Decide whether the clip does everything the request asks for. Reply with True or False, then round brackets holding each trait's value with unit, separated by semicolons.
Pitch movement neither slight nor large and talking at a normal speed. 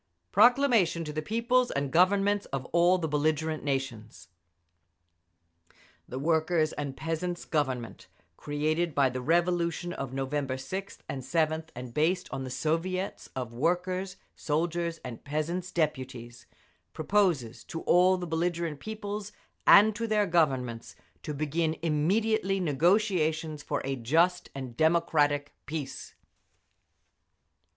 False (4.3 semitones; 120 wpm)